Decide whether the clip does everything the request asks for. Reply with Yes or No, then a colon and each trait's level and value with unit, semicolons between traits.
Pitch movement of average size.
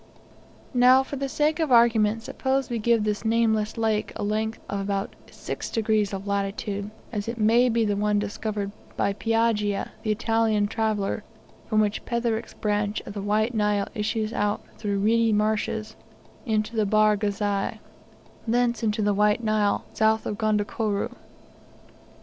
No: narrow, 1.7 semitones